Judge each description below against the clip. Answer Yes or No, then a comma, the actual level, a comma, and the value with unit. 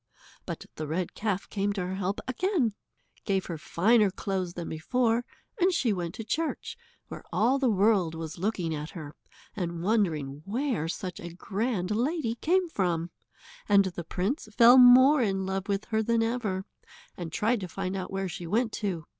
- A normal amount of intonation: Yes, average, 4.7 semitones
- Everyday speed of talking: Yes, average, 180 wpm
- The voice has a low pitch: No, high, 195 Hz